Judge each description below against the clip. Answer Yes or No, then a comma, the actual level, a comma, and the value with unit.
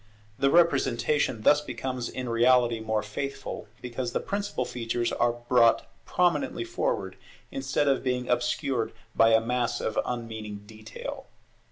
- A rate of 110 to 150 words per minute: Yes, slow, 135 wpm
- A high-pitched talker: No, low, 120 Hz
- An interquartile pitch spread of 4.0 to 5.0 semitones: No, average, 3.0 semitones